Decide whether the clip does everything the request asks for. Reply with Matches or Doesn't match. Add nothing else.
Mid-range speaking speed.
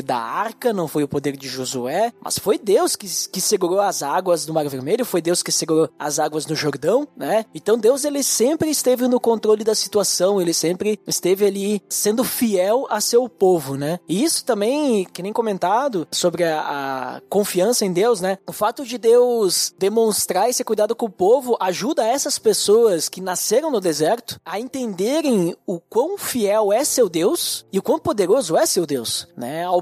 Doesn't match